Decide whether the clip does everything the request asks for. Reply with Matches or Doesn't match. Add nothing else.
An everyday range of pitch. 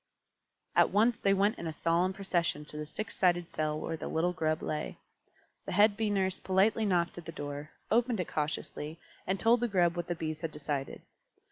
Matches